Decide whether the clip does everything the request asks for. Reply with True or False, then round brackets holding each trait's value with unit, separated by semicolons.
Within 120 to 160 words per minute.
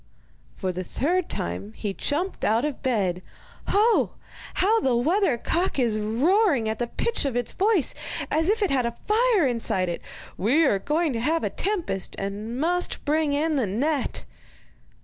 False (170 wpm)